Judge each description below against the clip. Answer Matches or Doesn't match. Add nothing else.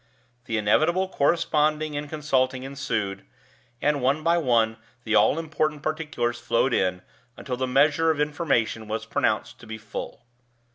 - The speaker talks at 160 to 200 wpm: Doesn't match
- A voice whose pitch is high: Doesn't match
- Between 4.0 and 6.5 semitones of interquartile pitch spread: Matches